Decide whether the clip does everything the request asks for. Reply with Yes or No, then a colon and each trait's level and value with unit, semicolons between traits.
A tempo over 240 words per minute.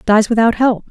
No: average, 200 wpm